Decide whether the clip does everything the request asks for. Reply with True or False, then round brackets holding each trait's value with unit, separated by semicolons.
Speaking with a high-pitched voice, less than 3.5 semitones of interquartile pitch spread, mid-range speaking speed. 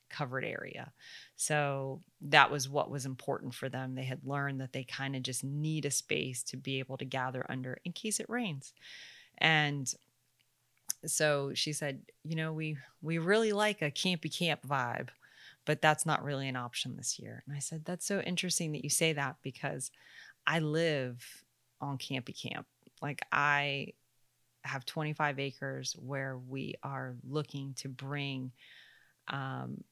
False (140 Hz; 2.9 semitones; 160 wpm)